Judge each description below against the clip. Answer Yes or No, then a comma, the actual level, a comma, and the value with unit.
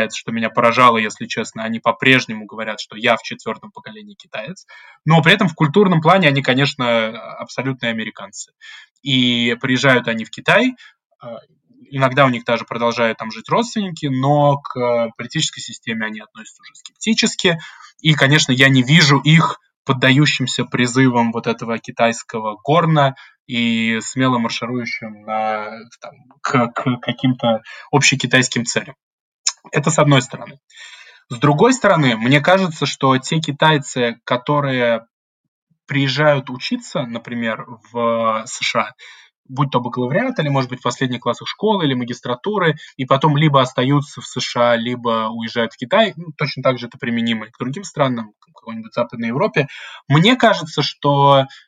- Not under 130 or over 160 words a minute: Yes, average, 145 wpm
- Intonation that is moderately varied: Yes, average, 4.2 semitones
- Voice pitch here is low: Yes, low, 130 Hz